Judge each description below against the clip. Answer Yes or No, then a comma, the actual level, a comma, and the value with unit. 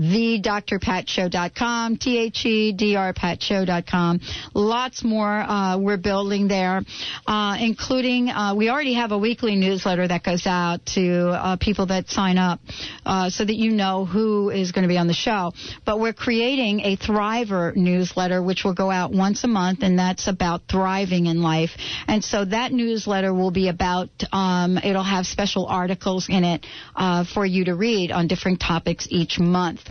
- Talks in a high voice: Yes, high, 195 Hz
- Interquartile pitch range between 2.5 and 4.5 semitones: Yes, average, 2.8 semitones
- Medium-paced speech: Yes, average, 165 wpm